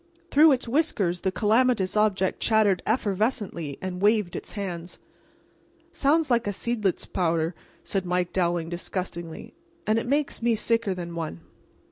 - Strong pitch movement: No, average, 4.6 semitones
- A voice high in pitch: Yes, high, 200 Hz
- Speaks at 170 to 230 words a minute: No, average, 140 wpm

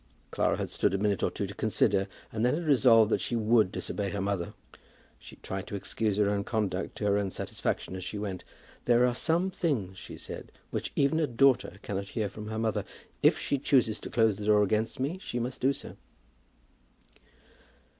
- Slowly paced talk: No, fast, 205 wpm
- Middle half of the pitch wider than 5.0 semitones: No, average, 3.7 semitones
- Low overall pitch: Yes, low, 110 Hz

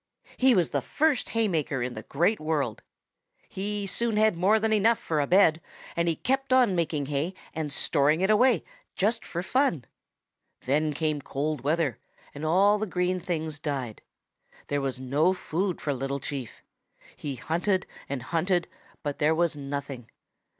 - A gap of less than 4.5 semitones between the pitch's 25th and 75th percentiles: No, wide, 5.6 semitones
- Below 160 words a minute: No, average, 165 wpm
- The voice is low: No, medium, 165 Hz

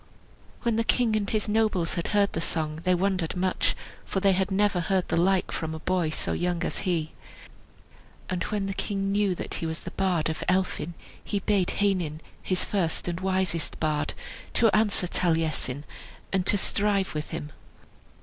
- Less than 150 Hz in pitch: No, medium, 185 Hz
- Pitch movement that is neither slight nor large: Yes, average, 3.3 semitones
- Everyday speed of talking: Yes, average, 180 wpm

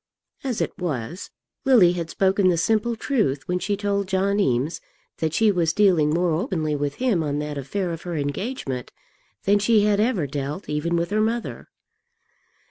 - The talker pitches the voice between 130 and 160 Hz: No, medium, 180 Hz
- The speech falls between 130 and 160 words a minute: No, average, 175 wpm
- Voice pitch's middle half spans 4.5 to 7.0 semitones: Yes, average, 5.3 semitones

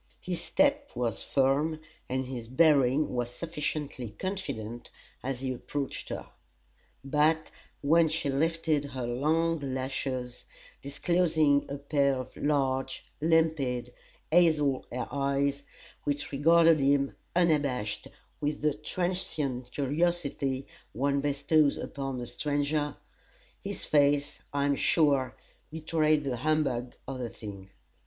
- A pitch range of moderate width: Yes, average, 3.1 semitones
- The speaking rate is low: Yes, slow, 115 wpm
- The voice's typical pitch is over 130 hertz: Yes, medium, 140 Hz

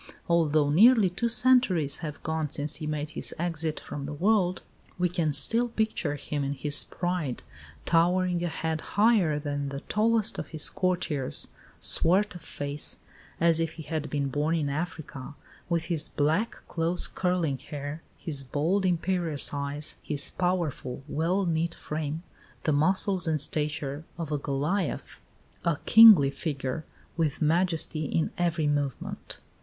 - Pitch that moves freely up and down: No, average, 3.4 semitones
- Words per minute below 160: Yes, average, 150 wpm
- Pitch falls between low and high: Yes, medium, 160 Hz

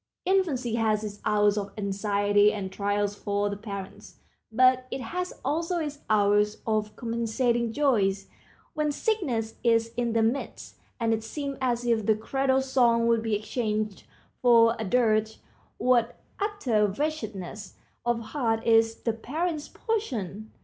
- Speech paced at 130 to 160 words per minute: Yes, average, 140 wpm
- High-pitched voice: Yes, high, 225 Hz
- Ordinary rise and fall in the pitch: Yes, average, 3.5 semitones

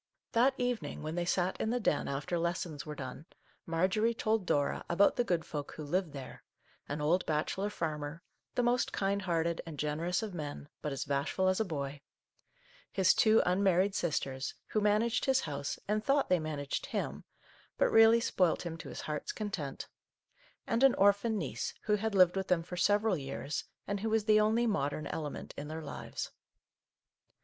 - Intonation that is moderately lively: No, wide, 5.8 semitones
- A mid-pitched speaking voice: Yes, medium, 180 Hz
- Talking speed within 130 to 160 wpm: No, average, 185 wpm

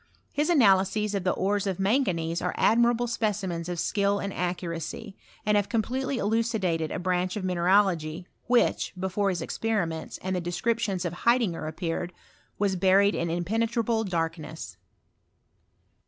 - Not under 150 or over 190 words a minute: No, average, 140 wpm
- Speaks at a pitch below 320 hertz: Yes, high, 190 Hz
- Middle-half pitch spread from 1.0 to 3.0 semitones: No, average, 4.0 semitones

